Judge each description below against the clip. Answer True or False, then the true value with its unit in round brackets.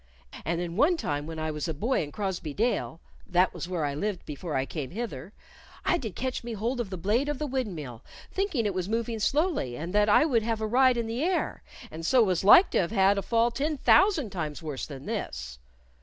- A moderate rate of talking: False (230 wpm)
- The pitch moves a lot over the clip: True (6.9 semitones)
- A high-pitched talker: True (205 Hz)